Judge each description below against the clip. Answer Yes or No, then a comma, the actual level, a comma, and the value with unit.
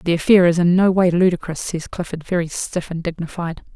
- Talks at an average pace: No, fast, 210 wpm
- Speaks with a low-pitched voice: No, medium, 175 Hz